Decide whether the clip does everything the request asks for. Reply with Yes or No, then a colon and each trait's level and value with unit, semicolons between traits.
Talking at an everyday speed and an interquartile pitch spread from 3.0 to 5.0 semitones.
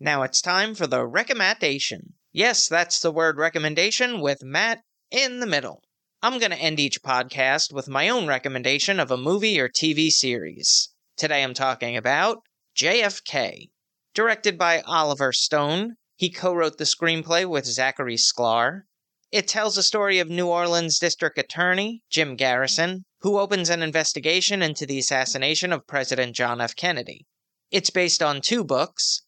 No: average, 160 wpm; wide, 5.4 semitones